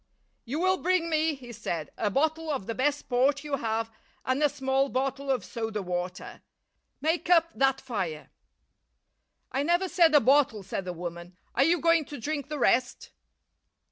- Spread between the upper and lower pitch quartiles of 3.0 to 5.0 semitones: No, wide, 5.6 semitones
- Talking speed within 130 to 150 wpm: No, average, 175 wpm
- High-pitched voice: Yes, very high, 270 Hz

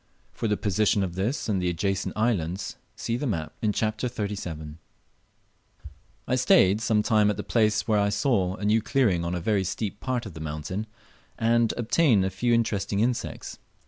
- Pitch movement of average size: Yes, average, 3.3 semitones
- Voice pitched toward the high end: No, low, 105 Hz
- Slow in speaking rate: No, average, 180 wpm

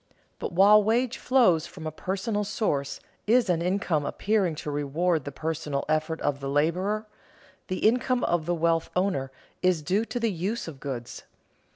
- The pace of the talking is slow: No, average, 170 wpm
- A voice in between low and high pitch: Yes, medium, 175 Hz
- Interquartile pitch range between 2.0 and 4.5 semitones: No, average, 5.2 semitones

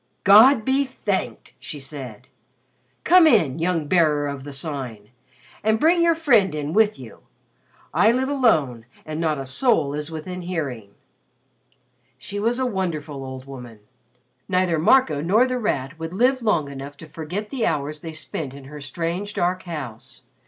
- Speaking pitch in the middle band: Yes, medium, 160 Hz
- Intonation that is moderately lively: No, wide, 7.1 semitones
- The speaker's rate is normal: Yes, average, 160 wpm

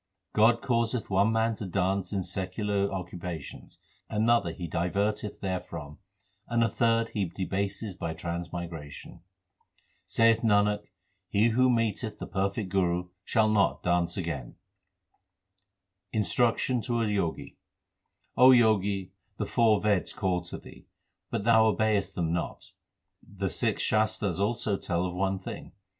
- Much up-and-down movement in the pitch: No, average, 3.7 semitones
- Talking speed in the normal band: No, slow, 130 wpm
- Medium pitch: No, low, 100 Hz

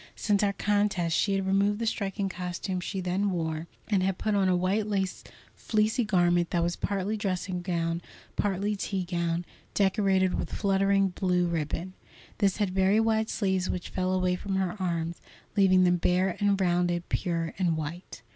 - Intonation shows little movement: Yes, narrow, 2.1 semitones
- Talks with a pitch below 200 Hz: Yes, medium, 185 Hz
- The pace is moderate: Yes, average, 175 wpm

